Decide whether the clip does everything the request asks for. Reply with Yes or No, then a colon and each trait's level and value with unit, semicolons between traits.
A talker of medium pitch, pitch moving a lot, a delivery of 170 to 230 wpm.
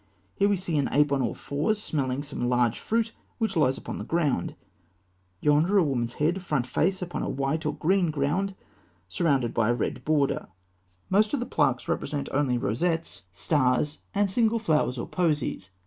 Yes: medium, 150 Hz; wide, 5.8 semitones; average, 180 wpm